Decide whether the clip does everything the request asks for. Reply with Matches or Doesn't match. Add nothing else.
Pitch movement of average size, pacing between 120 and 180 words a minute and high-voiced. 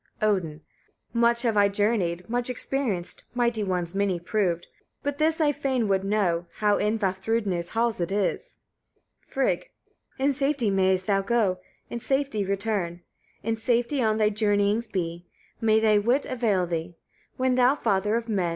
Matches